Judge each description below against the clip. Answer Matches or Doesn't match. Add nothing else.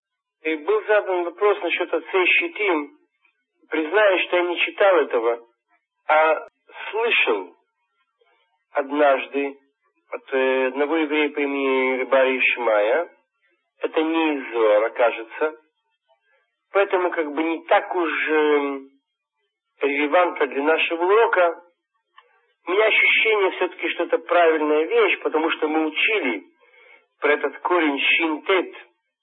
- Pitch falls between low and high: Matches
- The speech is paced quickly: Doesn't match